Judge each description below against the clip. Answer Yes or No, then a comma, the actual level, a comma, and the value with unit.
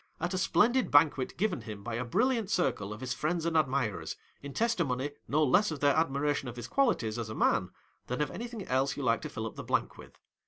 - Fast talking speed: Yes, fast, 240 wpm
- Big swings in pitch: Yes, wide, 6.1 semitones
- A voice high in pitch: No, medium, 145 Hz